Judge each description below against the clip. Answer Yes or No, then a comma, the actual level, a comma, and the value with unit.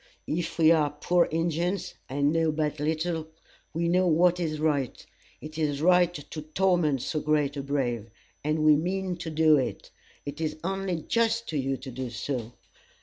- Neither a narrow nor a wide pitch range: Yes, average, 3.0 semitones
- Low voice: No, medium, 155 Hz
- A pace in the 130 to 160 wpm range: No, average, 175 wpm